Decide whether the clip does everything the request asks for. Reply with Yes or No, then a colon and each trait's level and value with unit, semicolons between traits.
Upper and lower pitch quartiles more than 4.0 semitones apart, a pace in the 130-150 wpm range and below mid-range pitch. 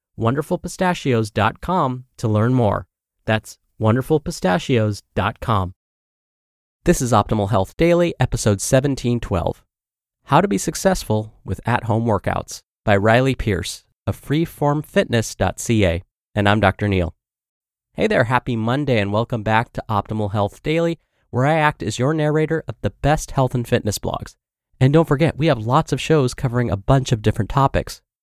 Yes: wide, 5.5 semitones; average, 145 wpm; low, 120 Hz